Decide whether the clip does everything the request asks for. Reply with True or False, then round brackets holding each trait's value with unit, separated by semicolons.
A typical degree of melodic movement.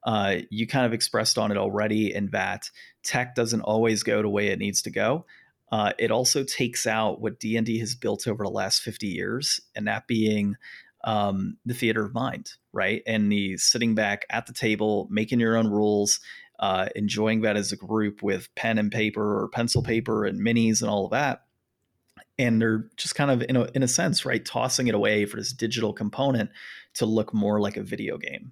False (2.0 semitones)